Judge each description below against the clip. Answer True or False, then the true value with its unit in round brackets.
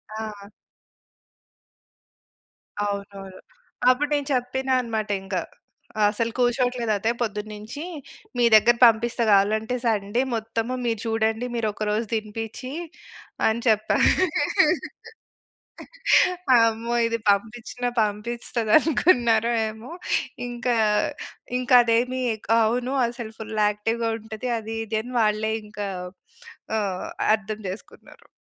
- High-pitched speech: True (225 Hz)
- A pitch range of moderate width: False (2.0 semitones)